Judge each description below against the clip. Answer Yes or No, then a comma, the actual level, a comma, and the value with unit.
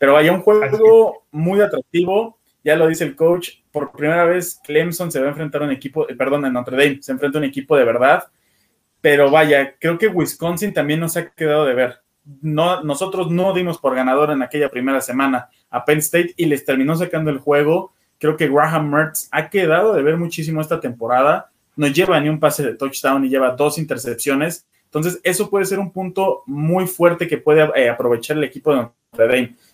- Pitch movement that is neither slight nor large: Yes, average, 3.4 semitones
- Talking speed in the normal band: No, fast, 205 wpm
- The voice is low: No, medium, 155 Hz